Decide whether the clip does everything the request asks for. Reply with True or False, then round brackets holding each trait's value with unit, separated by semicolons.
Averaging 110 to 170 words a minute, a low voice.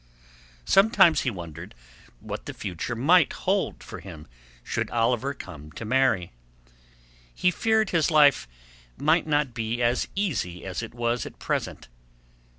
True (140 wpm; 120 Hz)